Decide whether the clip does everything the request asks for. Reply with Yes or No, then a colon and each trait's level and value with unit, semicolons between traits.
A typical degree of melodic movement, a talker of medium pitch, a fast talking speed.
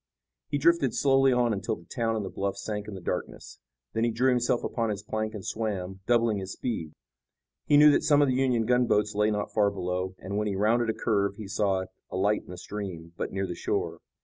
No: average, 3.7 semitones; low, 105 Hz; fast, 230 wpm